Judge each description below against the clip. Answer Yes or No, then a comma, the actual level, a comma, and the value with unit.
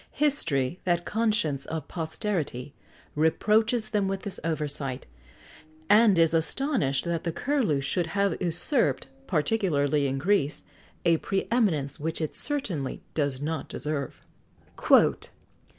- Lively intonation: Yes, wide, 6.1 semitones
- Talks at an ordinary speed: No, slow, 120 wpm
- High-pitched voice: No, medium, 165 Hz